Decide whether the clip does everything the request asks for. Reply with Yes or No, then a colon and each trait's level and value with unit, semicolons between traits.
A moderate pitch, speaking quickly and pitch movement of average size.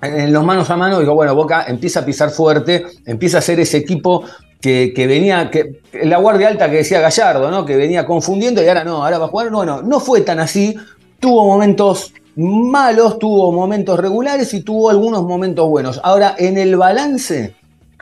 Yes: medium, 180 Hz; fast, 195 wpm; average, 4.6 semitones